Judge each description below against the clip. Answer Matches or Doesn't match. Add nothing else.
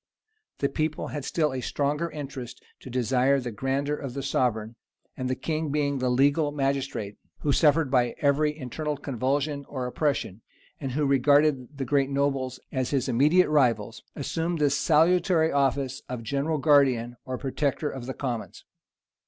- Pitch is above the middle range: Doesn't match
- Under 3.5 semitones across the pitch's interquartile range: Matches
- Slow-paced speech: Doesn't match